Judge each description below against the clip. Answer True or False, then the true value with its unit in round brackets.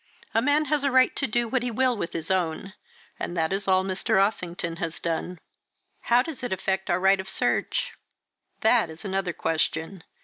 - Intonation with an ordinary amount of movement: False (5.7 semitones)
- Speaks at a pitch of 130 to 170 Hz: False (190 Hz)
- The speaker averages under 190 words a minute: False (195 wpm)